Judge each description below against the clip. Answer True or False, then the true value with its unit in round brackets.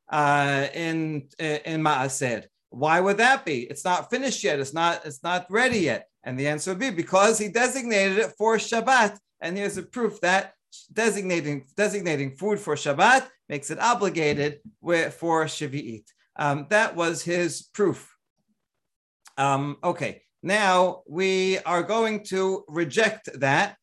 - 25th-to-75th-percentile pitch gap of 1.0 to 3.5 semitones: False (5.6 semitones)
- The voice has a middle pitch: True (175 Hz)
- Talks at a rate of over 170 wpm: False (145 wpm)